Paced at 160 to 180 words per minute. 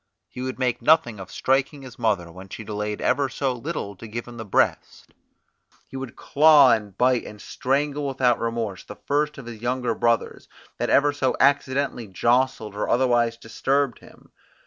Yes: average, 175 wpm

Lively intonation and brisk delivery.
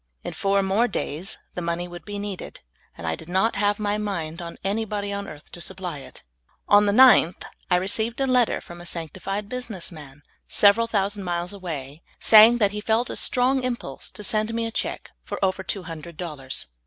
No: average, 3.8 semitones; fast, 220 wpm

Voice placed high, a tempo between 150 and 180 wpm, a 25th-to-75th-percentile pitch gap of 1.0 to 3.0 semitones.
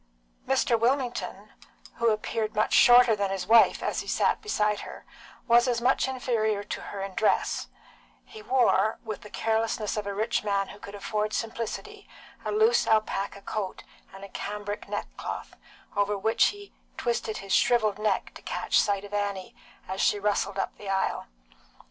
Yes: high, 215 Hz; average, 165 wpm; narrow, 2.6 semitones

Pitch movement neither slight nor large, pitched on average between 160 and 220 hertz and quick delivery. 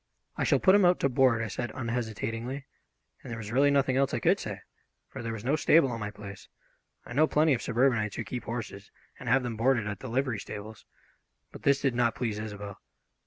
No: average, 3.5 semitones; low, 120 Hz; fast, 220 wpm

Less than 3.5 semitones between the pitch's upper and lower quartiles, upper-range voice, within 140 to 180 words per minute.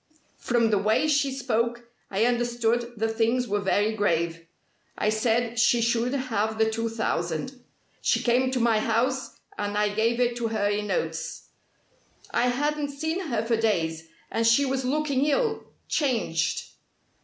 Yes: average, 2.8 semitones; high, 230 Hz; average, 155 wpm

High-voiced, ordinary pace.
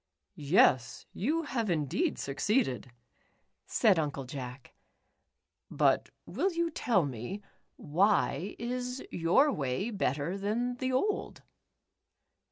No: high, 200 Hz; slow, 100 wpm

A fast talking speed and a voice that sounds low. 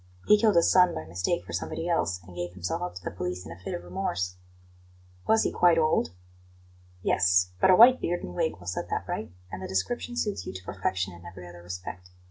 Yes: fast, 230 wpm; very low, 90 Hz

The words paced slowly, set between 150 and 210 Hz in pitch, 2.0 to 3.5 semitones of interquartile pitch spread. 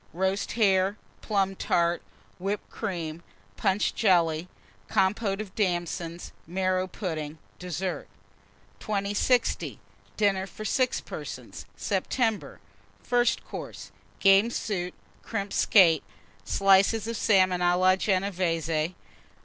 Yes: slow, 100 wpm; high, 190 Hz; narrow, 2.6 semitones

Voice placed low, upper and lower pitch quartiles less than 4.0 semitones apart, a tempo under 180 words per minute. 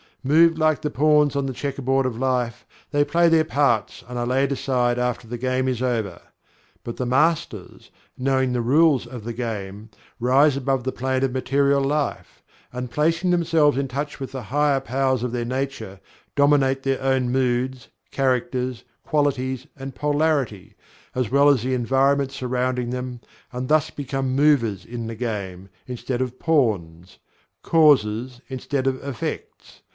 Yes: low, 130 Hz; narrow, 2.5 semitones; average, 160 wpm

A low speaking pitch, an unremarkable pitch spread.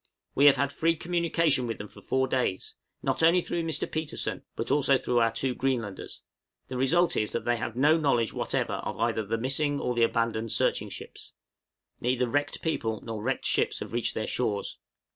Yes: low, 130 Hz; average, 4.1 semitones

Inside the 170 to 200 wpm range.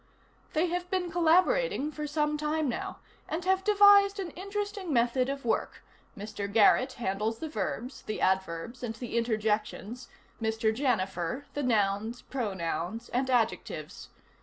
No: slow, 135 wpm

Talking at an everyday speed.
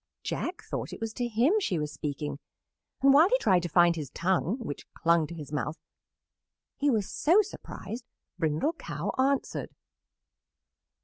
Yes: average, 160 wpm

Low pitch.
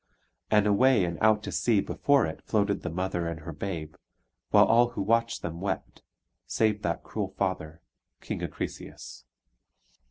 Yes: low, 100 Hz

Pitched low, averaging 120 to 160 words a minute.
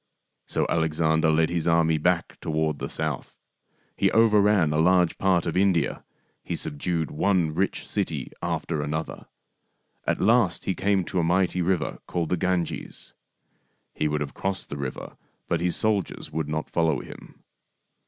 Yes: very low, 85 Hz; average, 155 wpm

